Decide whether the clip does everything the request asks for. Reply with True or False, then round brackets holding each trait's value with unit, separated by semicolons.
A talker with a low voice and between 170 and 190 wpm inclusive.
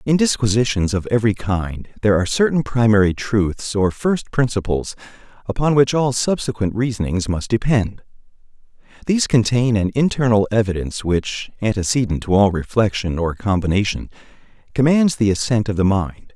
False (110 Hz; 140 wpm)